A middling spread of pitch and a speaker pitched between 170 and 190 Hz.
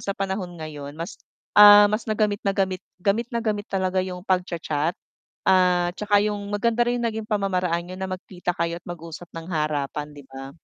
Yes: average, 3.4 semitones; medium, 185 Hz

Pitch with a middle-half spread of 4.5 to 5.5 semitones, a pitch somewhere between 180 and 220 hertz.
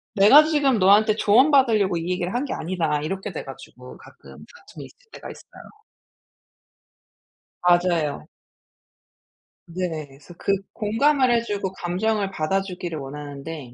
Yes: average, 5.2 semitones; medium, 185 Hz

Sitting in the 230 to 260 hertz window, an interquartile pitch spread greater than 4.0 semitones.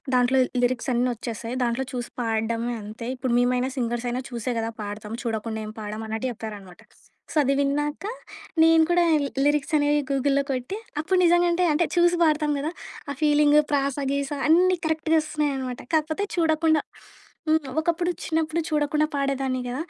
No: very high, 280 Hz; average, 4.5 semitones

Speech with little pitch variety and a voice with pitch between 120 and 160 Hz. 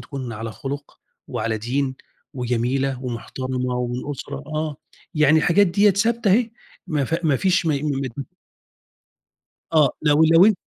No: average, 4.2 semitones; medium, 140 Hz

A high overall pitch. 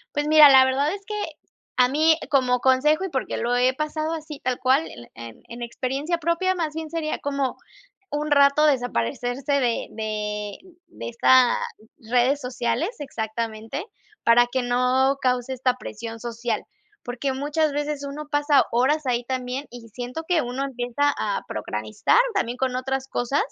Yes: very high, 260 Hz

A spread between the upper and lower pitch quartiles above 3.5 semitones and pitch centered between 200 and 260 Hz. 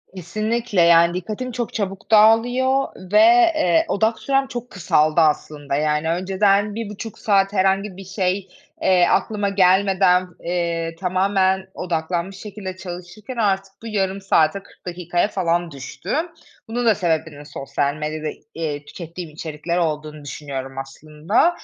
No: average, 4.1 semitones; medium, 185 Hz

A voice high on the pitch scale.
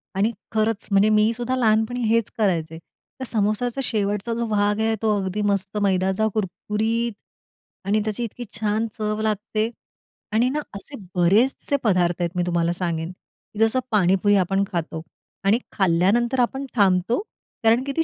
Yes: high, 215 Hz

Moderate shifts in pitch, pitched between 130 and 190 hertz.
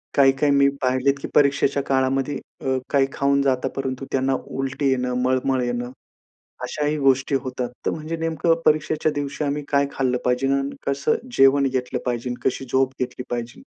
No: narrow, 1.5 semitones; low, 135 Hz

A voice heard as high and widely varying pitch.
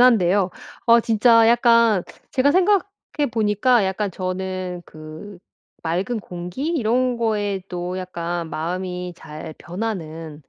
No: high, 195 Hz; average, 4.7 semitones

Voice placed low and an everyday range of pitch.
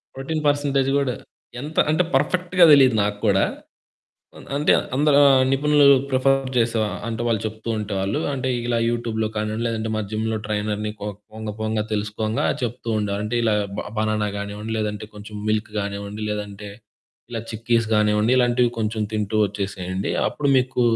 Yes: low, 110 Hz; average, 3.4 semitones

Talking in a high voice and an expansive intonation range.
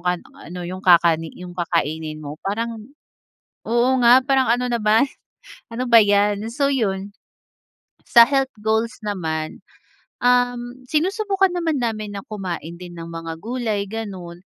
Yes: high, 215 Hz; wide, 5.7 semitones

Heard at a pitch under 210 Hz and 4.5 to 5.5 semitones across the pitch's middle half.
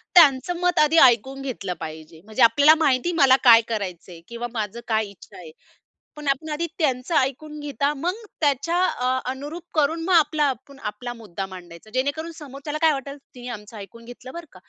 No: very high, 265 Hz; average, 5.0 semitones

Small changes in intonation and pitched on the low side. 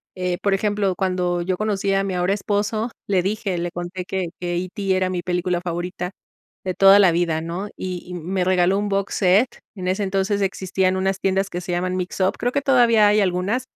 No: narrow, 1.9 semitones; medium, 185 Hz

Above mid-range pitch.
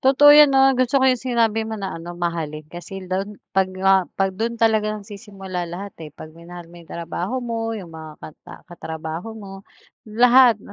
Yes: high, 195 Hz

